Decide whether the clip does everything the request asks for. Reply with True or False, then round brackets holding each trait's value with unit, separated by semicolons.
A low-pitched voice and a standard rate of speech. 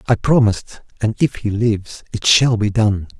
True (110 Hz; 190 wpm)